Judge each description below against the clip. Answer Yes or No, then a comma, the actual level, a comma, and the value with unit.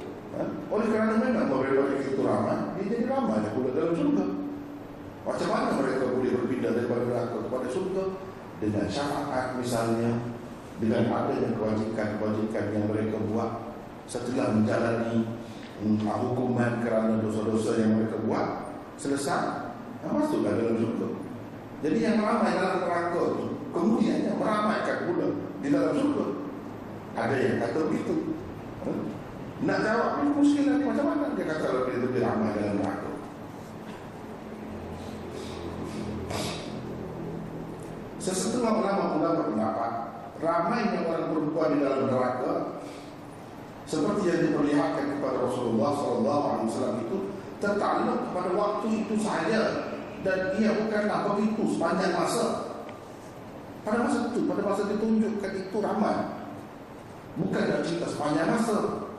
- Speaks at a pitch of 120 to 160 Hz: Yes, low, 135 Hz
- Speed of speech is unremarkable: Yes, average, 125 wpm